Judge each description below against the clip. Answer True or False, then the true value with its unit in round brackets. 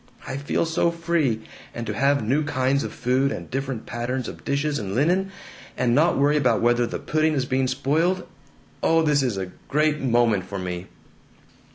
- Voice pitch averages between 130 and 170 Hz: True (135 Hz)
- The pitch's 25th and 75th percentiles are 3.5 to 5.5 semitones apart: True (4.1 semitones)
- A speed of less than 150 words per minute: False (185 wpm)